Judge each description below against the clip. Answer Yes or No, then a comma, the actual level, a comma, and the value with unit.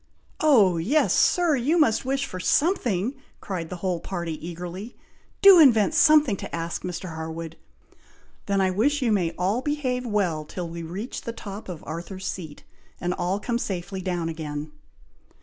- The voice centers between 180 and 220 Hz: Yes, high, 190 Hz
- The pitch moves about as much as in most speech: No, wide, 6.5 semitones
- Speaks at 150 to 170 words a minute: Yes, average, 165 wpm